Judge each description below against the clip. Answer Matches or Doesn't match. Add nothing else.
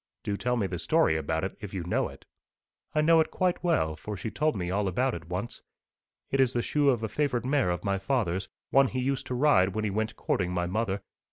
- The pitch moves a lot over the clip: Matches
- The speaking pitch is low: Matches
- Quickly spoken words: Matches